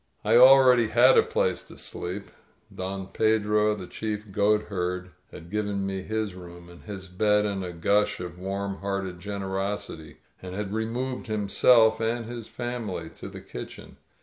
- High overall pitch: No, low, 100 Hz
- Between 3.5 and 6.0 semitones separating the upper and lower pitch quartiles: No, average, 2.8 semitones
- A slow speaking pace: No, average, 155 wpm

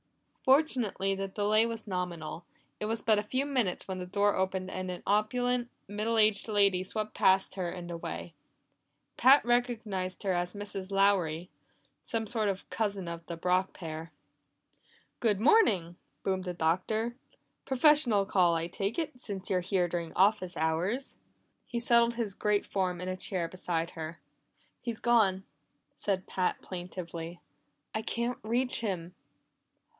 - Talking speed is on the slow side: No, average, 150 wpm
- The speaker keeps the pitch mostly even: No, average, 3.7 semitones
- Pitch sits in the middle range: No, high, 195 Hz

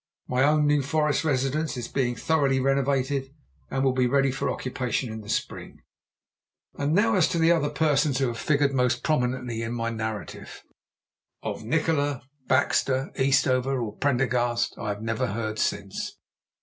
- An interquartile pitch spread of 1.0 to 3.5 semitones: Yes, average, 3.0 semitones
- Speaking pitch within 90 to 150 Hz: Yes, low, 135 Hz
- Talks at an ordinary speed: Yes, average, 160 wpm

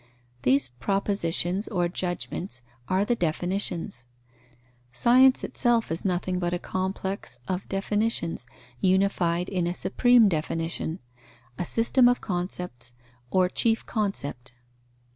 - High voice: No, medium, 180 Hz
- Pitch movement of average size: Yes, average, 3.2 semitones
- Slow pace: Yes, slow, 110 wpm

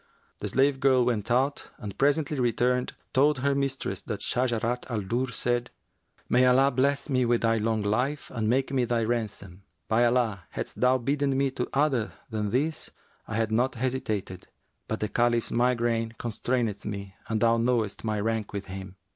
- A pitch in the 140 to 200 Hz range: No, low, 120 Hz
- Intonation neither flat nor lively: Yes, average, 3.0 semitones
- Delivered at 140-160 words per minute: No, average, 175 wpm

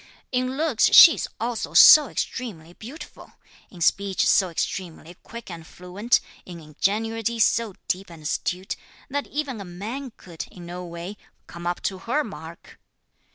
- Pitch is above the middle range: Yes, high, 195 Hz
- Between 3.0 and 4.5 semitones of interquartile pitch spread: No, average, 5.2 semitones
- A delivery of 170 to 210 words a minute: No, average, 155 wpm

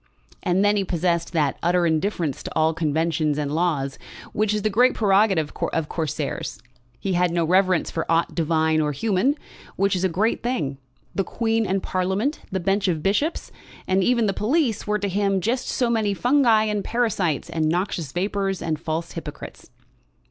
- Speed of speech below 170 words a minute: No, average, 175 wpm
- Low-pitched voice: No, medium, 185 Hz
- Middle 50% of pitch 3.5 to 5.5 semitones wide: Yes, average, 4.4 semitones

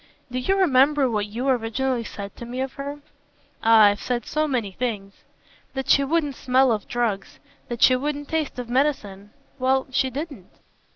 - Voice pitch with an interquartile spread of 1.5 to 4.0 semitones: Yes, average, 3.6 semitones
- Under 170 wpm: No, average, 175 wpm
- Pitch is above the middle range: Yes, very high, 255 Hz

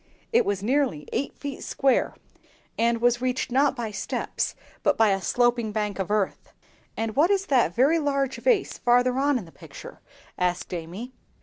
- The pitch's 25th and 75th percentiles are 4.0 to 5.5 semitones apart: Yes, average, 4.7 semitones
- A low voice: No, high, 245 Hz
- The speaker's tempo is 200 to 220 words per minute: No, average, 175 wpm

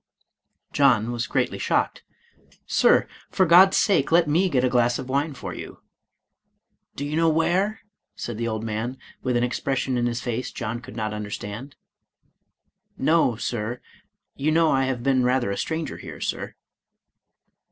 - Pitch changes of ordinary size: Yes, average, 4.6 semitones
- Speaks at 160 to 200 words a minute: Yes, average, 175 wpm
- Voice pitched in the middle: No, low, 130 Hz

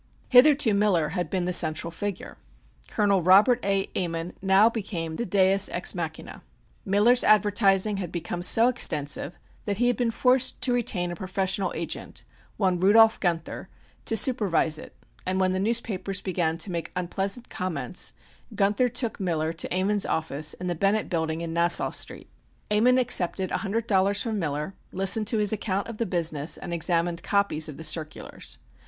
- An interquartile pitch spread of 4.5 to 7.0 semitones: No, average, 3.8 semitones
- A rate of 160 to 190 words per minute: Yes, average, 170 wpm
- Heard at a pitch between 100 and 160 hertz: No, high, 190 Hz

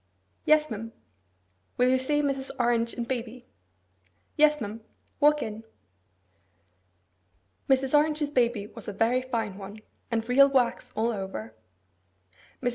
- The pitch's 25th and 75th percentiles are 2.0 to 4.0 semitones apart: Yes, average, 3.5 semitones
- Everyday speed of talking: No, slow, 125 wpm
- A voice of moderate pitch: No, high, 245 Hz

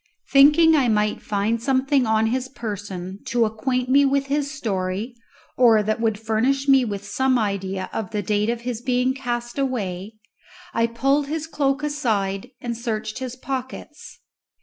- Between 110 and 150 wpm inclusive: No, average, 160 wpm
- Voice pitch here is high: Yes, high, 240 Hz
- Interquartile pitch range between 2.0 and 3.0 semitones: No, average, 4.0 semitones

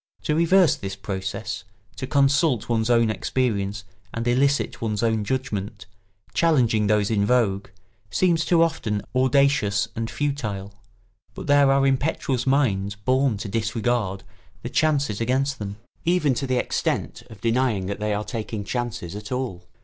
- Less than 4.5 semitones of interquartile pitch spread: No, average, 4.8 semitones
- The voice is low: Yes, low, 115 Hz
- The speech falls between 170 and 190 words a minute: No, average, 150 wpm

